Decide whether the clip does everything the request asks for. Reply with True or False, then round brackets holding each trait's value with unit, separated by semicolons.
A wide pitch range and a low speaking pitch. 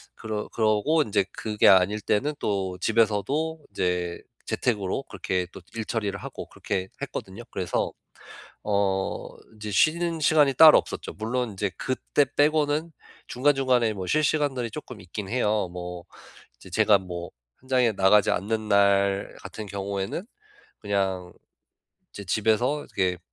False (5.0 semitones; 105 Hz)